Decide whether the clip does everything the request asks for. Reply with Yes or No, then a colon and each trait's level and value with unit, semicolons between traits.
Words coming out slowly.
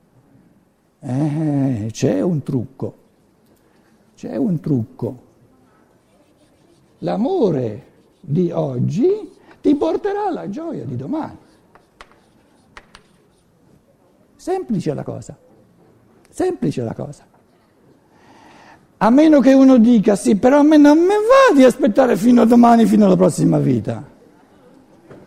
Yes: slow, 100 wpm